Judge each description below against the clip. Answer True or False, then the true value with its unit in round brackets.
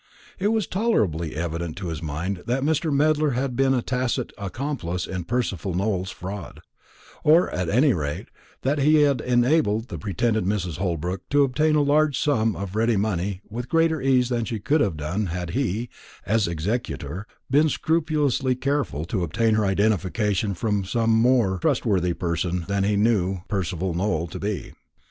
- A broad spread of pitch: True (6.6 semitones)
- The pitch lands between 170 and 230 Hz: False (110 Hz)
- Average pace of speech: True (165 wpm)